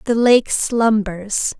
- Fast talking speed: No, slow, 115 wpm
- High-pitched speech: Yes, high, 220 Hz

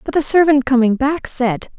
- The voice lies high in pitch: Yes, very high, 270 Hz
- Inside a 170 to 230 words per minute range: Yes, average, 200 wpm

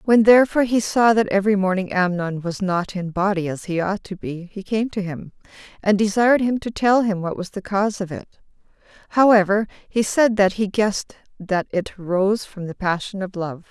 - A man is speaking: No, female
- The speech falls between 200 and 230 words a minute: Yes, fast, 205 wpm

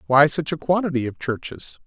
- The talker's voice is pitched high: No, medium, 150 Hz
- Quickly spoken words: No, average, 195 wpm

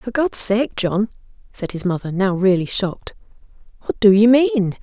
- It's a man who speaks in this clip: No, female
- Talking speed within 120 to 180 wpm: Yes, average, 175 wpm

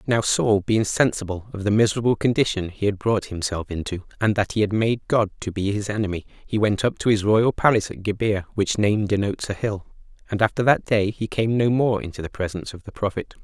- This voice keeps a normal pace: No, fast, 230 wpm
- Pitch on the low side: Yes, low, 105 Hz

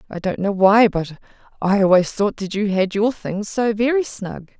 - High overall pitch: Yes, high, 205 Hz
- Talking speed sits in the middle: No, fast, 210 wpm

